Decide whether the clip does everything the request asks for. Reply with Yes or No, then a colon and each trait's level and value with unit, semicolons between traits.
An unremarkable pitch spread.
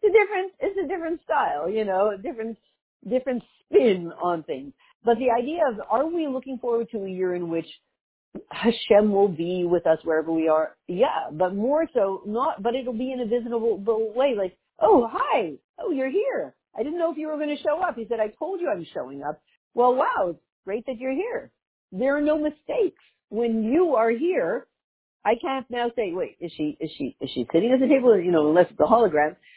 No: wide, 8.4 semitones